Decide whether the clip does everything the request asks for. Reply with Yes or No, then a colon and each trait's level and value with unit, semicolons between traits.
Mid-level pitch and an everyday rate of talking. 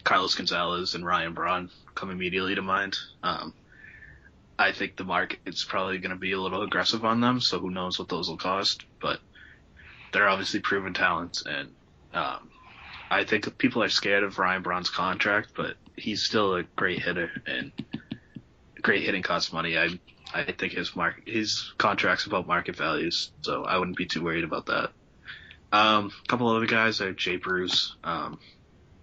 No: very low, 95 Hz; average, 175 wpm